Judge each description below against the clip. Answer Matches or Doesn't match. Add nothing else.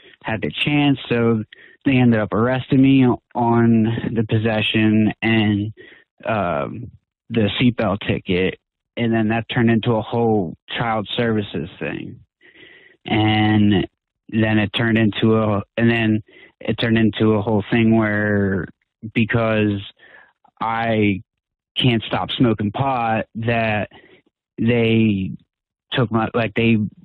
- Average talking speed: Doesn't match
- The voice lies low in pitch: Matches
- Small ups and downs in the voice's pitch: Matches